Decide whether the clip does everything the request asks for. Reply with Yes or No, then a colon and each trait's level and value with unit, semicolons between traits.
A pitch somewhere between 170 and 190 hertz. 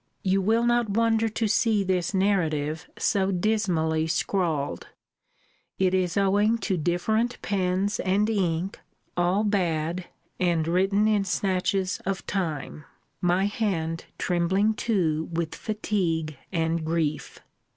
Yes: medium, 185 Hz